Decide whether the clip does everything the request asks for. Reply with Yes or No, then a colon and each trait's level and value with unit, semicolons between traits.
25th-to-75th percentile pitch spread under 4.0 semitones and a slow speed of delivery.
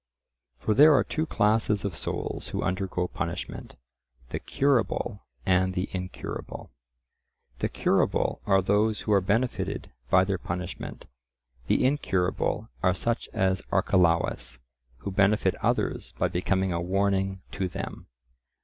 Yes: narrow, 2.5 semitones; slow, 125 wpm